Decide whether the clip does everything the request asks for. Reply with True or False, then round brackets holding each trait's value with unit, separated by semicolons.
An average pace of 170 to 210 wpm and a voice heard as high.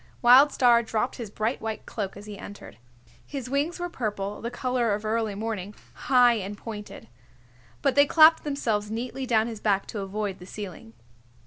True (180 wpm; 225 Hz)